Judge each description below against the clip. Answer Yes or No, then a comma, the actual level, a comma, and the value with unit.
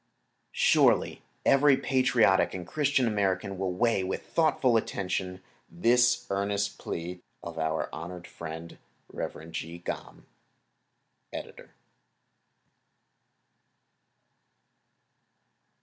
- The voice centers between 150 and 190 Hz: No, very low, 95 Hz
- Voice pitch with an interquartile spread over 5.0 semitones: Yes, wide, 5.6 semitones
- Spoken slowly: Yes, slow, 80 wpm